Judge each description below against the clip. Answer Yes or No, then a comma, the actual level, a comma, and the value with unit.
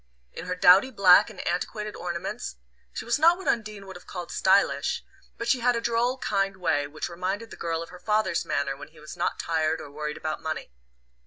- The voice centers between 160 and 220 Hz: Yes, medium, 185 Hz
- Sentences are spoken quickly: Yes, fast, 215 wpm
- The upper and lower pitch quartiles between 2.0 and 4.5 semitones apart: No, average, 5.0 semitones